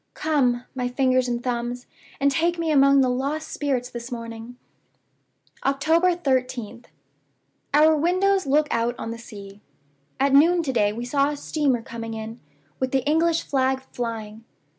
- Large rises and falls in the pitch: No, average, 3.9 semitones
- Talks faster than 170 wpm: No, average, 155 wpm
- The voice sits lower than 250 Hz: No, very high, 260 Hz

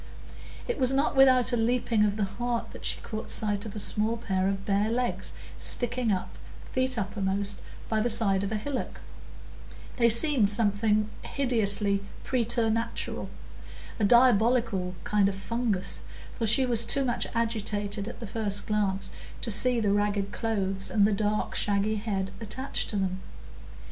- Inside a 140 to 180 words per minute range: Yes, average, 155 wpm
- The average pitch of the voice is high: Yes, high, 215 Hz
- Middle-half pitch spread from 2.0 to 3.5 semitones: Yes, average, 2.9 semitones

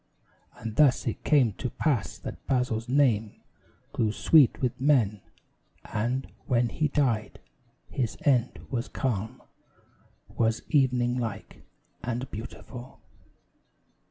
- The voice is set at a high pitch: No, low, 125 Hz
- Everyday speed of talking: No, slow, 110 wpm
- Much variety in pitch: No, average, 2.9 semitones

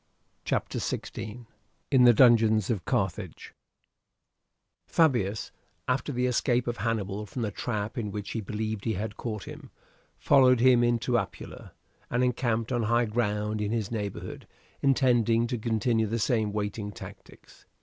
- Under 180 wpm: Yes, average, 145 wpm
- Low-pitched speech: Yes, low, 115 Hz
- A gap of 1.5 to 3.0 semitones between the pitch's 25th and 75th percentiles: Yes, narrow, 2.5 semitones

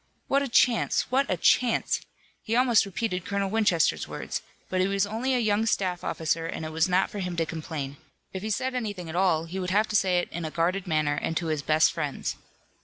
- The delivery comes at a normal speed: No, fast, 230 wpm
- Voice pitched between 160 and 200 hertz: Yes, medium, 185 Hz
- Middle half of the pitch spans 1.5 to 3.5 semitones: No, average, 4.7 semitones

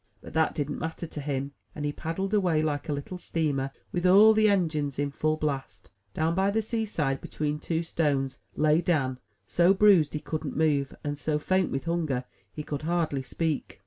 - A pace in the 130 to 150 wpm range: No, average, 190 wpm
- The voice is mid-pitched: Yes, medium, 155 Hz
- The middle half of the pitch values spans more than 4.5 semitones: No, average, 3.2 semitones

